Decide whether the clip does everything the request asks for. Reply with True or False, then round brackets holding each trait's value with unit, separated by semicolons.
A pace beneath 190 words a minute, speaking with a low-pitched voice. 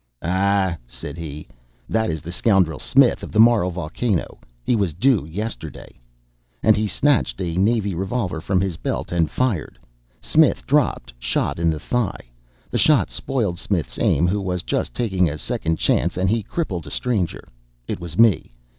True (170 wpm; 95 Hz)